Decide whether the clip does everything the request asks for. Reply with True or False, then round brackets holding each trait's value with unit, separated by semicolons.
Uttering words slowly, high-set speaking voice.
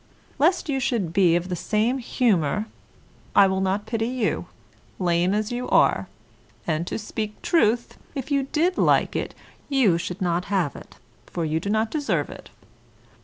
False (170 wpm; 210 Hz)